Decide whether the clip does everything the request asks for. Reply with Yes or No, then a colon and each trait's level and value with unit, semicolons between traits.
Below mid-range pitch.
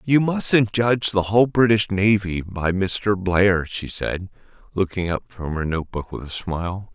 Yes: low, 100 Hz